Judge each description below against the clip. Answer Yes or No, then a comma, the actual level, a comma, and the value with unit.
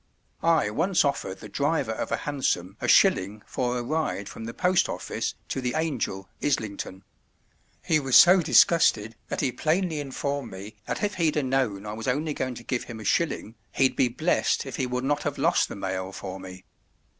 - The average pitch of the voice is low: Yes, low, 130 Hz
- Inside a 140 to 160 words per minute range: No, average, 200 wpm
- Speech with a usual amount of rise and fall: No, wide, 6.4 semitones